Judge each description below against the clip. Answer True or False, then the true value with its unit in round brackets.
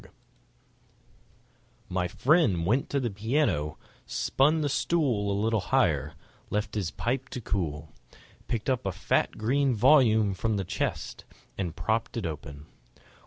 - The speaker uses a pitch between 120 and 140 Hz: False (110 Hz)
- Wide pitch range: True (6.5 semitones)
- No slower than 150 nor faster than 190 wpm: False (140 wpm)